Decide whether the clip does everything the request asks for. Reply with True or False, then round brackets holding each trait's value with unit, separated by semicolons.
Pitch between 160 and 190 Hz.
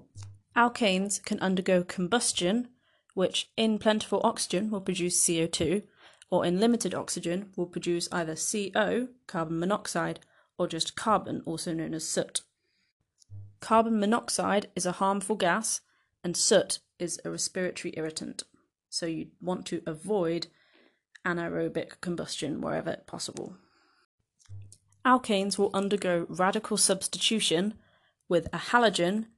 True (185 Hz)